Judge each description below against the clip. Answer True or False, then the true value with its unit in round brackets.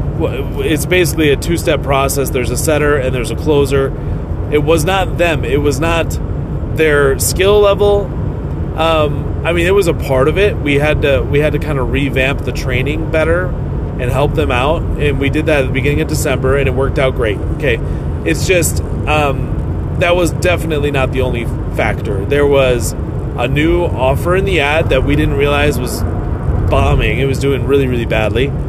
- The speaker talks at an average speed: True (190 wpm)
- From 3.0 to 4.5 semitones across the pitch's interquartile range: True (3.7 semitones)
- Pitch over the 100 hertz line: True (135 Hz)